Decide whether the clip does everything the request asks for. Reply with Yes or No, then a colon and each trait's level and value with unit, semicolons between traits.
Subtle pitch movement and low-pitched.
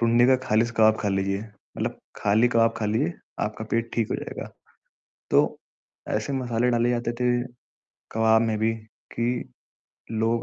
Yes: narrow, 1.7 semitones; low, 115 Hz